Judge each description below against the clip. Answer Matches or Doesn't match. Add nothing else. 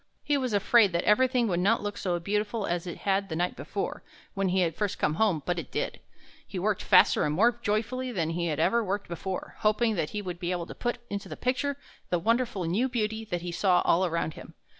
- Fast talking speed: Matches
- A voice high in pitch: Matches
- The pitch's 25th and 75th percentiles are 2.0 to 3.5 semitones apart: Doesn't match